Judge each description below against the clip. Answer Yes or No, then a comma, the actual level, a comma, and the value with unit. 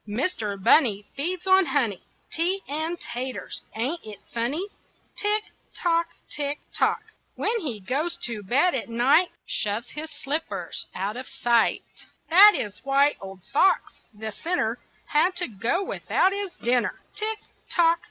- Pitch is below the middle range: No, very high, 285 Hz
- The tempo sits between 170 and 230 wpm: No, average, 140 wpm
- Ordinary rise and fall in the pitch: No, wide, 7.3 semitones